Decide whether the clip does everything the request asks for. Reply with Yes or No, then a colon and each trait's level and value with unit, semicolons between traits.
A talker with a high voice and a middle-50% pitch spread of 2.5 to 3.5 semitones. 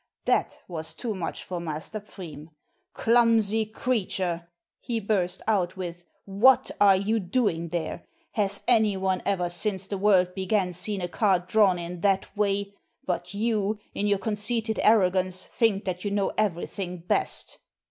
Yes: high, 195 Hz; average, 3.0 semitones